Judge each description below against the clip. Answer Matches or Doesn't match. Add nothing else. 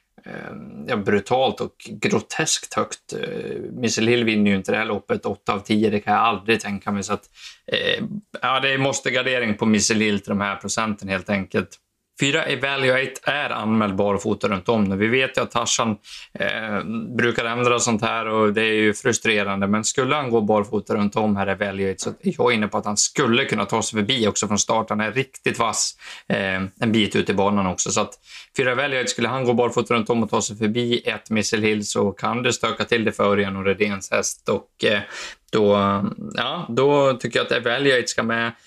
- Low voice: Matches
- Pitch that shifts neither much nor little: Matches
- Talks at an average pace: Doesn't match